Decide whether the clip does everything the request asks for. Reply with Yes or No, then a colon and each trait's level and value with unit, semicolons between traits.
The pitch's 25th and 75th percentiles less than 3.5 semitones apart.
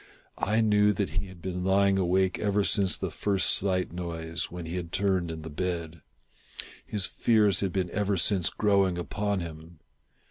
Yes: narrow, 2.6 semitones